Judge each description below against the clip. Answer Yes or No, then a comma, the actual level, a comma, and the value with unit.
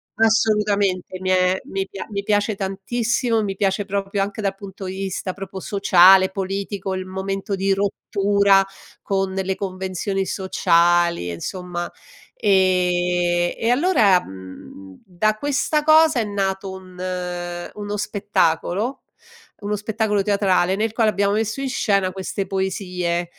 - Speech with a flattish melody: Yes, narrow, 1.8 semitones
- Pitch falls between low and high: No, high, 195 Hz